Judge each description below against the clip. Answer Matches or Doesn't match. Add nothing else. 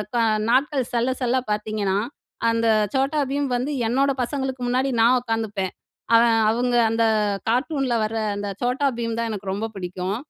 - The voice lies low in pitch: Doesn't match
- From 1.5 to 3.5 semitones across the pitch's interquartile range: Matches